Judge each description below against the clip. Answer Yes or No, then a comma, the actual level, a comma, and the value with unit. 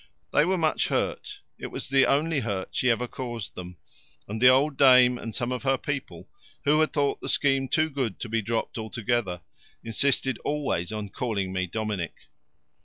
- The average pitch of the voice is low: Yes, low, 125 Hz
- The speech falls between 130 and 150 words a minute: No, average, 180 wpm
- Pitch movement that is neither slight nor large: Yes, average, 4.4 semitones